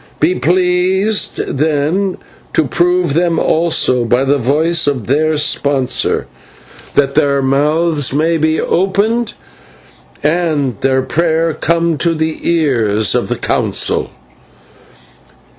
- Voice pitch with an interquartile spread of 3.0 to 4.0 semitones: Yes, average, 3.5 semitones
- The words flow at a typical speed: No, slow, 110 wpm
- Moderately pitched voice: Yes, medium, 155 Hz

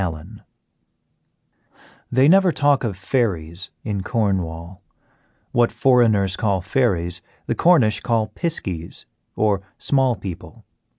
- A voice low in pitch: Yes, low, 105 Hz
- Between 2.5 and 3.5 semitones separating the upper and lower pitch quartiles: No, wide, 5.4 semitones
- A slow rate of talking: Yes, slow, 105 wpm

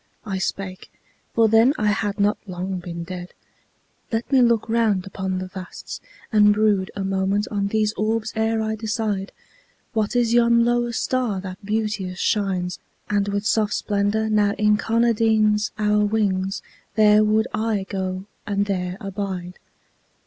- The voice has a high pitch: Yes, high, 210 Hz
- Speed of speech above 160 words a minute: No, average, 150 wpm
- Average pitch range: No, narrow, 2.3 semitones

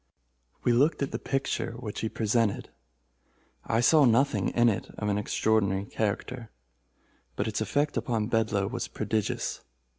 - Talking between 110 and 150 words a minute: Yes, average, 145 wpm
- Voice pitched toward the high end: No, low, 110 Hz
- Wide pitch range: No, average, 2.7 semitones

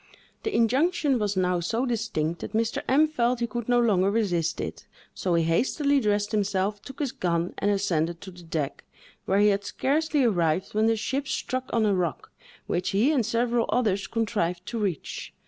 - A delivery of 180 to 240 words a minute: Yes, average, 190 wpm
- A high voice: Yes, high, 210 Hz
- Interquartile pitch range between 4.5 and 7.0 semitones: Yes, average, 4.9 semitones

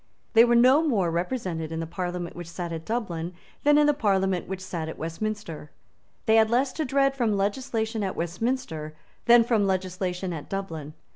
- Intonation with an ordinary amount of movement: No, wide, 5.7 semitones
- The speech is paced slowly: No, average, 185 wpm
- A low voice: No, high, 190 Hz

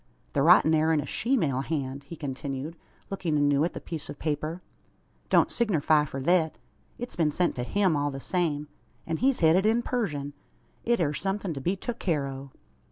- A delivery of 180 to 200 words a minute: Yes, average, 195 wpm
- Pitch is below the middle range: No, medium, 155 Hz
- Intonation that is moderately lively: Yes, average, 4.2 semitones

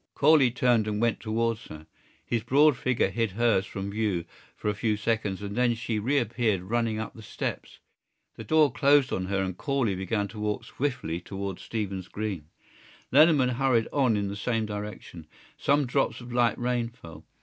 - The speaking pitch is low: Yes, low, 115 Hz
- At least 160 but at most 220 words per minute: Yes, average, 180 wpm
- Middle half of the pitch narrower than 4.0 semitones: Yes, average, 3.6 semitones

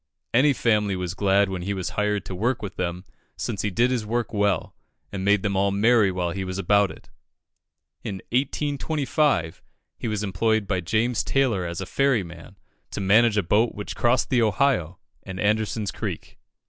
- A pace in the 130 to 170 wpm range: No, average, 185 wpm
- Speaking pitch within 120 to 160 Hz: No, low, 105 Hz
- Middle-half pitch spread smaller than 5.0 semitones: Yes, average, 3.8 semitones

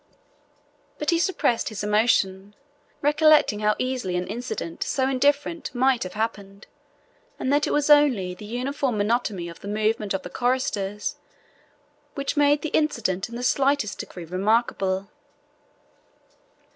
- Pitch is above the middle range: Yes, high, 230 Hz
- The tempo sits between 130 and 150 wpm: Yes, slow, 135 wpm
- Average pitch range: No, wide, 5.8 semitones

